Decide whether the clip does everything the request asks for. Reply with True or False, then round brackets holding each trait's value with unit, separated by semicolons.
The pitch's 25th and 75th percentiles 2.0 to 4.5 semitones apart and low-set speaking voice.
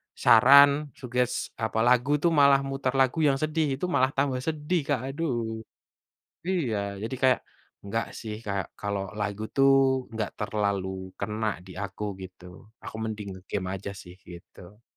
False (5.3 semitones; 115 Hz)